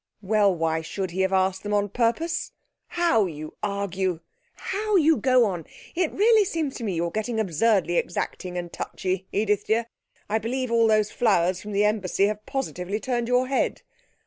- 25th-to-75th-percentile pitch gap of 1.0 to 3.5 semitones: No, average, 4.7 semitones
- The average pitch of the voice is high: Yes, high, 210 Hz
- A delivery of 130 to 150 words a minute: No, average, 175 wpm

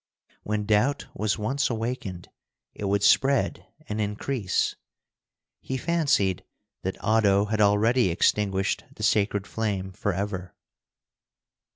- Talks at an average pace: No, slow, 105 wpm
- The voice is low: Yes, low, 105 Hz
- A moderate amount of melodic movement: No, narrow, 2.3 semitones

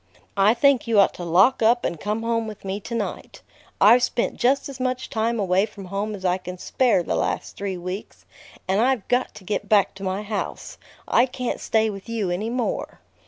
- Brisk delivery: Yes, fast, 210 wpm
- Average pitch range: Yes, average, 3.5 semitones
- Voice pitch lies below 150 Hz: No, high, 215 Hz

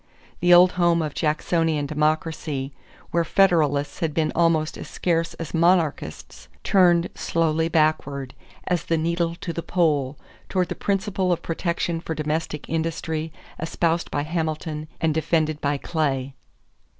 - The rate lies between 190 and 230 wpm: No, average, 140 wpm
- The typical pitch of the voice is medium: Yes, medium, 160 Hz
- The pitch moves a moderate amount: No, narrow, 1.9 semitones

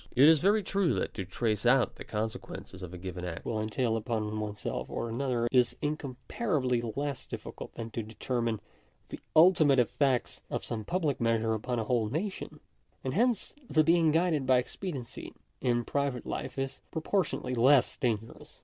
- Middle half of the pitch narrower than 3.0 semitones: No, average, 5.0 semitones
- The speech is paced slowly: No, average, 165 wpm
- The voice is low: Yes, low, 125 Hz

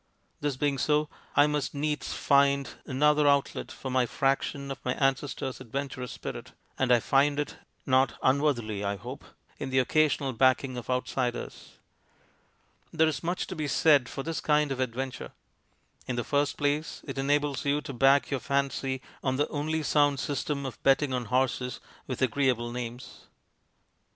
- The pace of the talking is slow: No, average, 160 wpm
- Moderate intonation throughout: No, narrow, 2.1 semitones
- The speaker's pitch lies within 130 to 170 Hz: Yes, low, 135 Hz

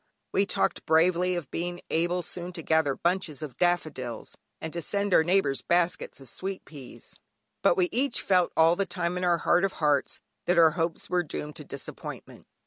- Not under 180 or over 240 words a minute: Yes, average, 190 wpm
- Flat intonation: Yes, narrow, 2.2 semitones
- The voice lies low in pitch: No, medium, 175 Hz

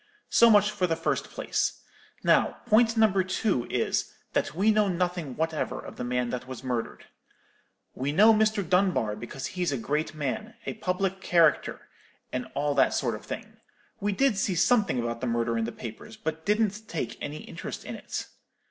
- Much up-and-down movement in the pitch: Yes, wide, 8.2 semitones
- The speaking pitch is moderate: Yes, medium, 175 Hz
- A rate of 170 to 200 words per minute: Yes, average, 185 wpm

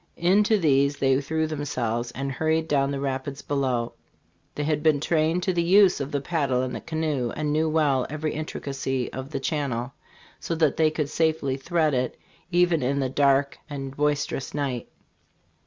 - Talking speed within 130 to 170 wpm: No, average, 180 wpm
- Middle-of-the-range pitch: Yes, medium, 145 Hz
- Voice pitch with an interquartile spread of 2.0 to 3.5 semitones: Yes, average, 2.8 semitones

